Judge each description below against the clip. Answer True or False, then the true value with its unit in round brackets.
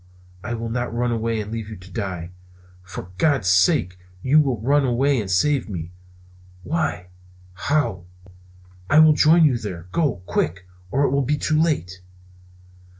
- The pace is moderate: True (160 wpm)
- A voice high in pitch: False (115 Hz)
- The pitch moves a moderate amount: False (7.5 semitones)